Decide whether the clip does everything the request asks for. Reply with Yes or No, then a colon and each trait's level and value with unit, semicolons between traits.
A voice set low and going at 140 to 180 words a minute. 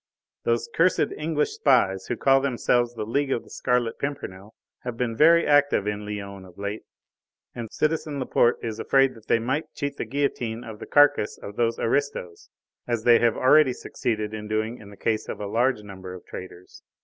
No: low, 115 Hz; average, 190 wpm